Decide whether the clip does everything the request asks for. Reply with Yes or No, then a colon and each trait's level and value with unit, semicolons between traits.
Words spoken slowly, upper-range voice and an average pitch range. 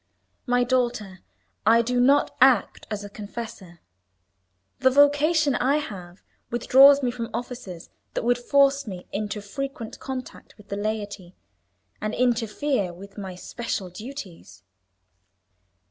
Yes: slow, 125 wpm; high, 230 Hz; average, 4.5 semitones